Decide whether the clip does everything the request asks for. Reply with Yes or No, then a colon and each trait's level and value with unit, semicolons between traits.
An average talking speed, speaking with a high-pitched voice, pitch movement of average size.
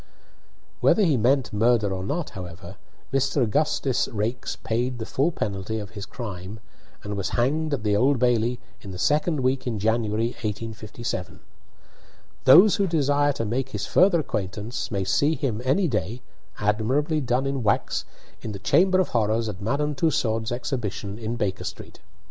No: average, 160 wpm; low, 120 Hz; average, 4.7 semitones